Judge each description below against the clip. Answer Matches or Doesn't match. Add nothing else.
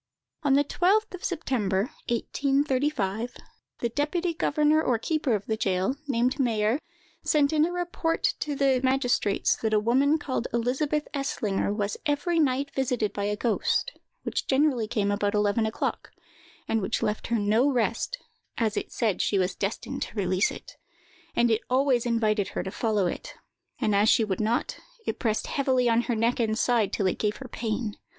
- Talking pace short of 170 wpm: Doesn't match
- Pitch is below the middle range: Doesn't match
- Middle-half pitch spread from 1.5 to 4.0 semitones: Doesn't match